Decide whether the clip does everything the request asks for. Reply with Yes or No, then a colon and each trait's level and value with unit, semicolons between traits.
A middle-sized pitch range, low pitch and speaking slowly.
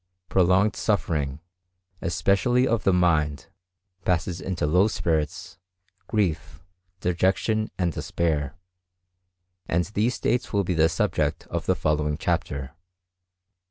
Yes: average, 4.3 semitones; very low, 90 Hz; slow, 110 wpm